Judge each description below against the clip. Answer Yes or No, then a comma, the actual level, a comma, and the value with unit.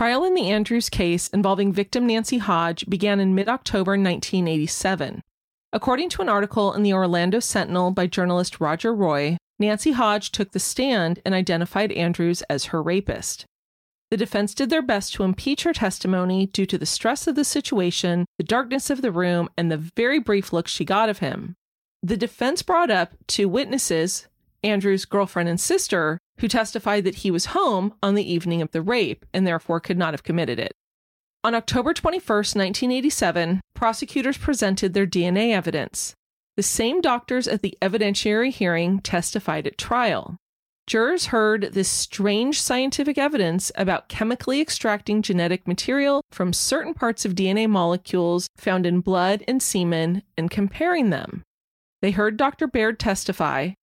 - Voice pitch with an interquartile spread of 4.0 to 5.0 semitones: Yes, average, 4.6 semitones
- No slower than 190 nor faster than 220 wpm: No, average, 165 wpm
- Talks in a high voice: Yes, high, 200 Hz